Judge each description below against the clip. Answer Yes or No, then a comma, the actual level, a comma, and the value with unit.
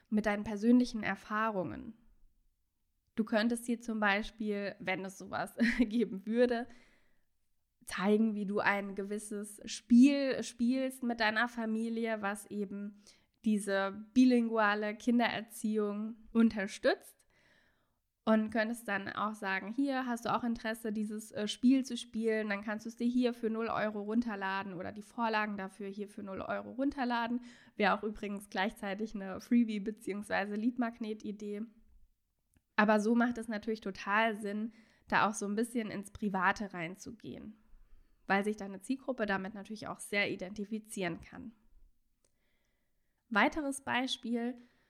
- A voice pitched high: Yes, high, 215 Hz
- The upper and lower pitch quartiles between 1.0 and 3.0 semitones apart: Yes, narrow, 2.4 semitones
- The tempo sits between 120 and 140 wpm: Yes, average, 130 wpm